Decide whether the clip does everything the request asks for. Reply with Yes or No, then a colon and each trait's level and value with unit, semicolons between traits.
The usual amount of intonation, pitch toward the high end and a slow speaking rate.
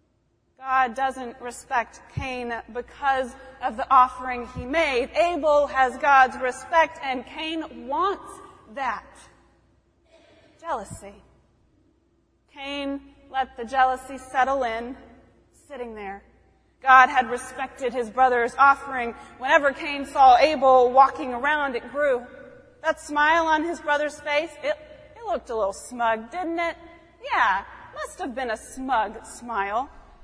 Yes: average, 3.0 semitones; very high, 265 Hz; slow, 125 wpm